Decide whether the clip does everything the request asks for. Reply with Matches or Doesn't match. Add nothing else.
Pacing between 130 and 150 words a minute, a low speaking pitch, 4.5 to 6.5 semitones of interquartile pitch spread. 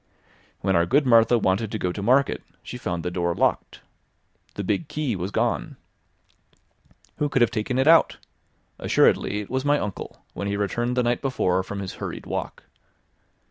Doesn't match